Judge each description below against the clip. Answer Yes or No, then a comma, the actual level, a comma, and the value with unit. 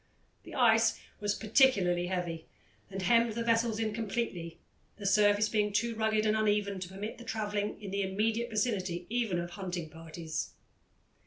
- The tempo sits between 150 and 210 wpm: Yes, average, 160 wpm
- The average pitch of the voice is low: No, high, 210 Hz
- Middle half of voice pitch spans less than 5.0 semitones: Yes, average, 3.2 semitones